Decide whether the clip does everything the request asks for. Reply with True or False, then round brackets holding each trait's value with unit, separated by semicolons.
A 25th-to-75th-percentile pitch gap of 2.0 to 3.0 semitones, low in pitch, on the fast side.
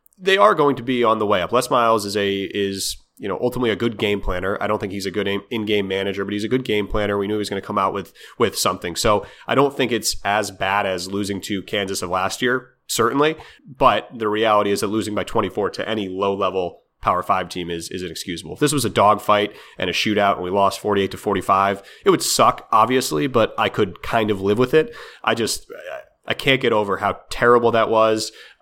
True (2.7 semitones; 105 Hz; 250 wpm)